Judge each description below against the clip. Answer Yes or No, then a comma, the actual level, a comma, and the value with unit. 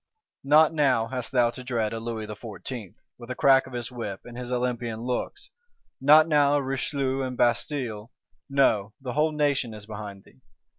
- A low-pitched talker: Yes, low, 125 Hz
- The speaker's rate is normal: Yes, average, 180 wpm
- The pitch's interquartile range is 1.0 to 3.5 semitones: Yes, average, 3.2 semitones